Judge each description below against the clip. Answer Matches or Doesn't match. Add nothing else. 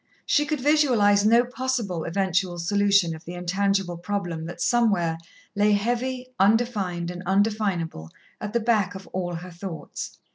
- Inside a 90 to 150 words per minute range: Matches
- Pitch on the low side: Doesn't match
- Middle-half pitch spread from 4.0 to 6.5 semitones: Matches